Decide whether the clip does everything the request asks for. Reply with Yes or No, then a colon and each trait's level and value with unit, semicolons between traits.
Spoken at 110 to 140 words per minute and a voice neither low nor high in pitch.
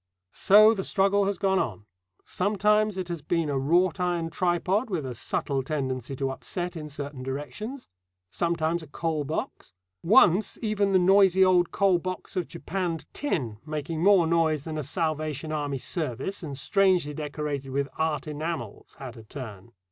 No: average, 165 wpm; medium, 165 Hz